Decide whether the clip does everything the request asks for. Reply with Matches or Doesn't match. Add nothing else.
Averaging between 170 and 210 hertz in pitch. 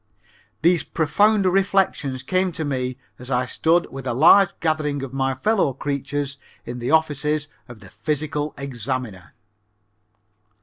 Doesn't match